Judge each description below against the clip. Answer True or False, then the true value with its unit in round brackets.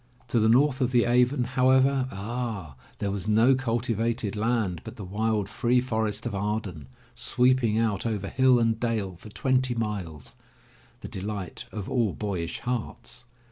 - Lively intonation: False (3.3 semitones)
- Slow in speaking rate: False (160 wpm)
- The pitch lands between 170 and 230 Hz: False (115 Hz)